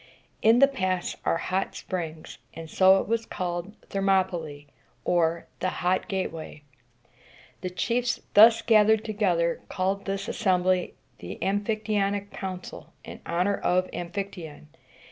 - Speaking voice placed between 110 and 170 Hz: No, high, 190 Hz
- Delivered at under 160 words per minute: Yes, average, 145 wpm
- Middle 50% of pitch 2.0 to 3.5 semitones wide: Yes, average, 2.7 semitones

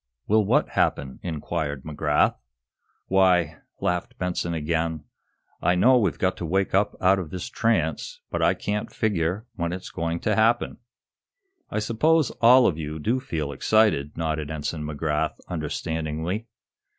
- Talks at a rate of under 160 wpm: Yes, average, 145 wpm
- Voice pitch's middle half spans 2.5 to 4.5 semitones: No, average, 5.1 semitones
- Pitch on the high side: No, very low, 85 Hz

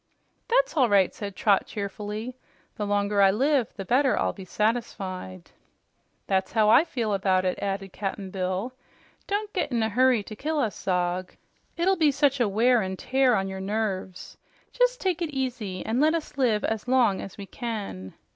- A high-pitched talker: Yes, high, 215 Hz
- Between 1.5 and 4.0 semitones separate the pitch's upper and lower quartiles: No, average, 5.1 semitones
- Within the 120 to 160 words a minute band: No, average, 185 wpm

